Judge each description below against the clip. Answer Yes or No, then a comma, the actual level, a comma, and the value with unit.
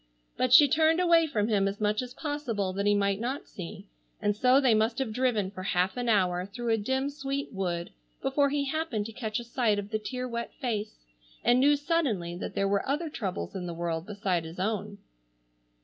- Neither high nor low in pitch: No, high, 220 Hz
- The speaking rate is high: Yes, fast, 210 wpm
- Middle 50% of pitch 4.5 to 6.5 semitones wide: Yes, average, 5.2 semitones